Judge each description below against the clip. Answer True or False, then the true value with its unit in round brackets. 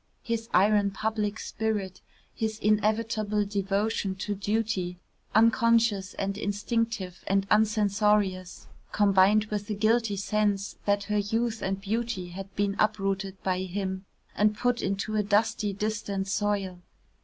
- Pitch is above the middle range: True (205 Hz)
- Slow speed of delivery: True (125 wpm)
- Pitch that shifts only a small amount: True (1.8 semitones)